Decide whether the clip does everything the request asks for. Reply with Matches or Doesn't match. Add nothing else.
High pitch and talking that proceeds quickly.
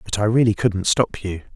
Doesn't match